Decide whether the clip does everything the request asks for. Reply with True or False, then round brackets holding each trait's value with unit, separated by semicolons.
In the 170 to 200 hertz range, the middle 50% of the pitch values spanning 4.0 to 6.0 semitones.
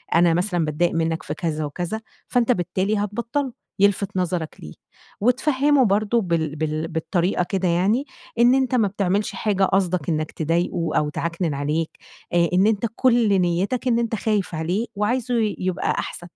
True (185 Hz; 4.8 semitones)